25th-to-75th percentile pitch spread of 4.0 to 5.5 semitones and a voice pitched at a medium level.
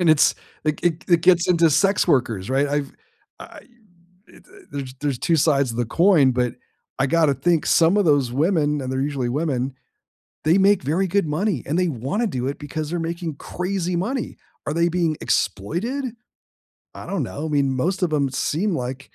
Yes: average, 4.5 semitones; medium, 155 Hz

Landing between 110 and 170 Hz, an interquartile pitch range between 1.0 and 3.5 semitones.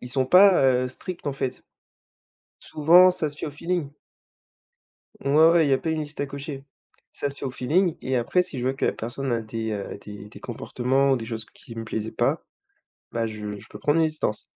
No: low, 135 Hz; average, 4.8 semitones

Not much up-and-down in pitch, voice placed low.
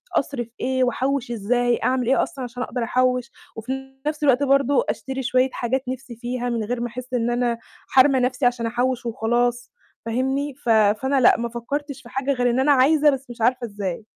No: narrow, 1.9 semitones; very high, 250 Hz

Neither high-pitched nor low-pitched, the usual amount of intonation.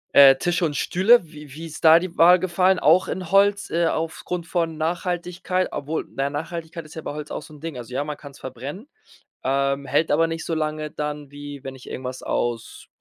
Yes: medium, 160 Hz; average, 3.4 semitones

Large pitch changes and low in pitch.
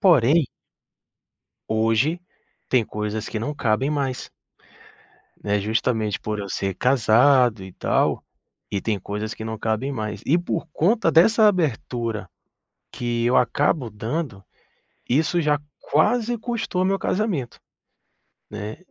Yes: wide, 6.7 semitones; low, 120 Hz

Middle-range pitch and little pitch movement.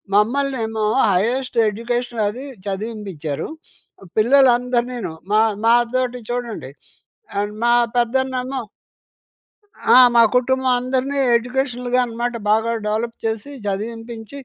No: high, 240 Hz; narrow, 2.3 semitones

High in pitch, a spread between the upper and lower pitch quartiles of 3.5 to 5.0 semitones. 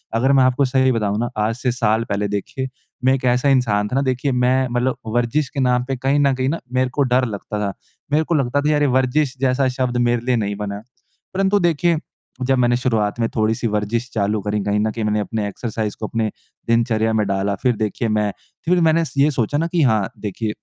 No: low, 120 Hz; average, 3.8 semitones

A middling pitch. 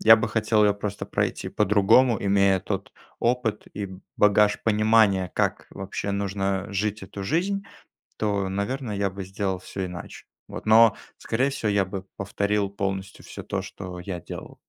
No: low, 100 Hz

